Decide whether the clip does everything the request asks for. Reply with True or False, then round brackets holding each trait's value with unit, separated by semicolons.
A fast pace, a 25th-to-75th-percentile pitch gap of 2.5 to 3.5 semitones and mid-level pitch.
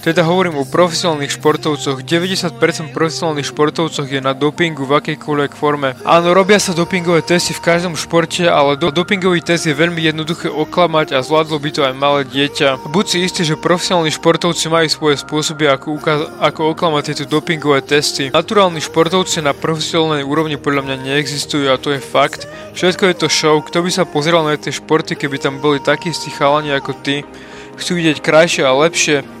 True (180 wpm; 2.8 semitones; 155 Hz)